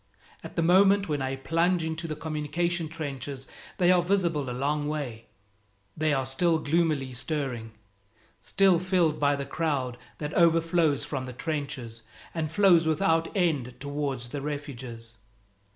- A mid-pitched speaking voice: Yes, medium, 150 Hz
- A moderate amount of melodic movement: Yes, average, 3.7 semitones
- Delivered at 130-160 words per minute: Yes, average, 145 wpm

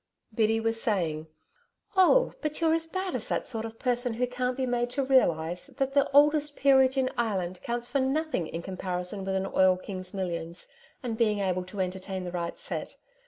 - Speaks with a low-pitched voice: No, high, 225 Hz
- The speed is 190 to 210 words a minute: Yes, average, 195 wpm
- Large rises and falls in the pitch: Yes, wide, 6.2 semitones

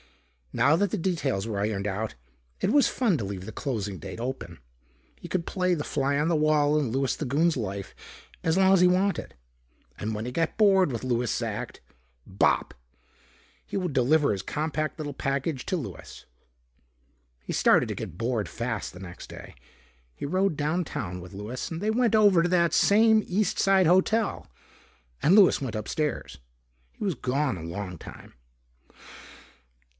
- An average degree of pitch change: No, wide, 8.4 semitones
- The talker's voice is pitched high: No, medium, 145 Hz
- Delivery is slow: No, average, 170 wpm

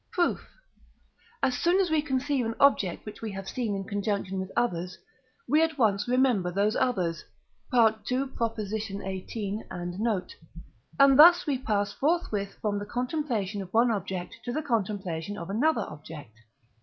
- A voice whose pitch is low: No, high, 215 Hz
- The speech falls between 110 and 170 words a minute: Yes, average, 155 wpm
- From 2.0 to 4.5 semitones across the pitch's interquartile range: No, average, 5.0 semitones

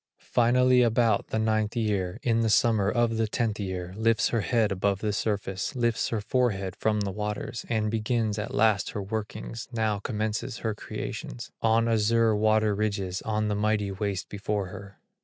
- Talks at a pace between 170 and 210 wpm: Yes, average, 175 wpm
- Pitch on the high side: No, low, 110 Hz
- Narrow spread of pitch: Yes, narrow, 1.9 semitones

